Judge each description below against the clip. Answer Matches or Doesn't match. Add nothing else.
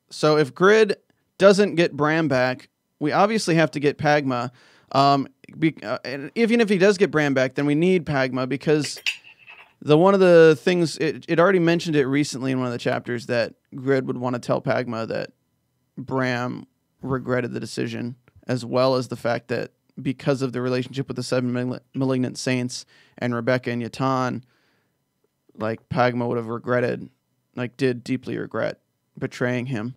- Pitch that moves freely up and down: Doesn't match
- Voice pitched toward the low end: Matches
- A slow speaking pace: Doesn't match